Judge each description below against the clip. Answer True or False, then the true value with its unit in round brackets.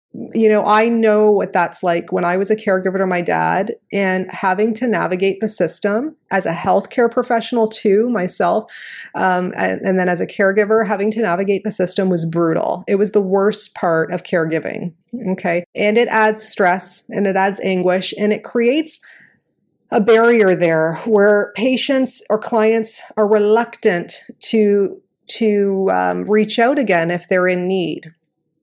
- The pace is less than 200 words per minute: True (165 wpm)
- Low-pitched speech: False (205 Hz)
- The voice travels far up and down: False (3.3 semitones)